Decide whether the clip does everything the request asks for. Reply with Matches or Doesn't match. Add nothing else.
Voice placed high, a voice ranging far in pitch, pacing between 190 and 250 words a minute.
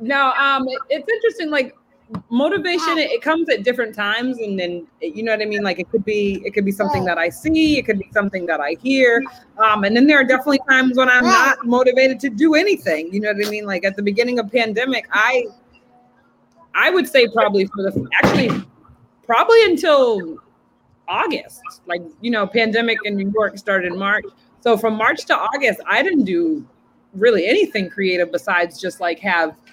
Matches